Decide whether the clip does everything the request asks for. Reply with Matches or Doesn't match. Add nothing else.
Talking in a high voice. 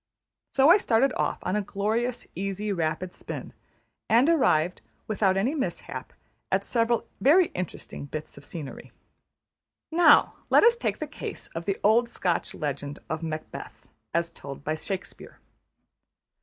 Matches